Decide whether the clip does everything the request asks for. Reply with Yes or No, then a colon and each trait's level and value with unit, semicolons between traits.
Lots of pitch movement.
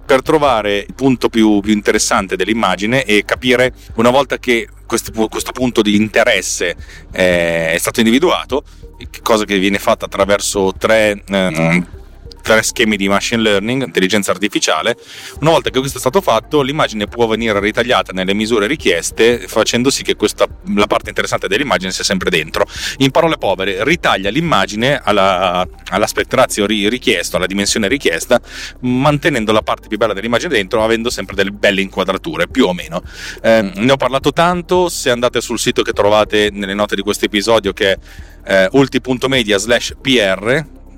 No: average, 3.8 semitones